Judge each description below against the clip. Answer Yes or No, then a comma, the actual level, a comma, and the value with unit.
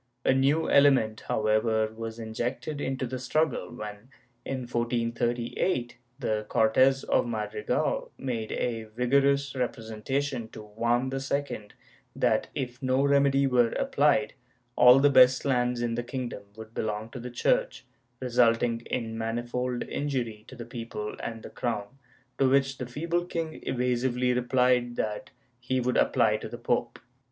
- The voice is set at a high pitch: No, low, 125 Hz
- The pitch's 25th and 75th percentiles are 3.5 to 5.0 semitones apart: No, average, 2.7 semitones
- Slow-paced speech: No, average, 145 wpm